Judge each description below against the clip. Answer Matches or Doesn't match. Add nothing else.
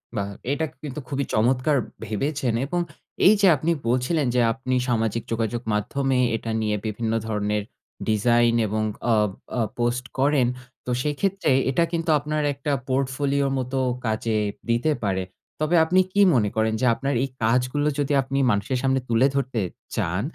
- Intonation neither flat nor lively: Matches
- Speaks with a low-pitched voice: Matches